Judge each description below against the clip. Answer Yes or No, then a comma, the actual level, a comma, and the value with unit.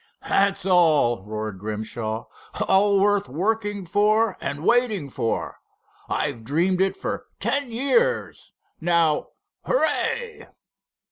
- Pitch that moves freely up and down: Yes, wide, 7.7 semitones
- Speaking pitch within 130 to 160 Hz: No, high, 190 Hz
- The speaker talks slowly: Yes, slow, 90 wpm